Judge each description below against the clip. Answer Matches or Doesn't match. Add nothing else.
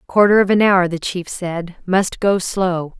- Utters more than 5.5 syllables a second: Doesn't match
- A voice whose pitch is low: Doesn't match